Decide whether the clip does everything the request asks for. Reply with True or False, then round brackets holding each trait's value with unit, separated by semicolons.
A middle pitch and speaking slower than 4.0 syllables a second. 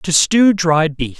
True (170 Hz; 3.5 syllables/s)